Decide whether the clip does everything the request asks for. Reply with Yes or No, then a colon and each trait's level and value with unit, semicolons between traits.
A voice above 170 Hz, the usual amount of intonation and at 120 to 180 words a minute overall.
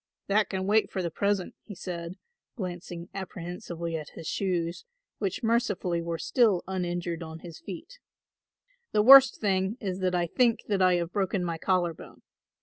Yes: medium, 185 Hz; average, 3.0 semitones; average, 165 wpm